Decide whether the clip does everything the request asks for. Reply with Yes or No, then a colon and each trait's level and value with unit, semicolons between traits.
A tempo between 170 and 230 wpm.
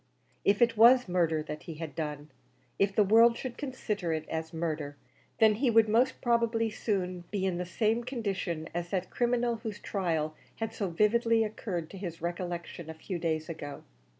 Yes: average, 180 wpm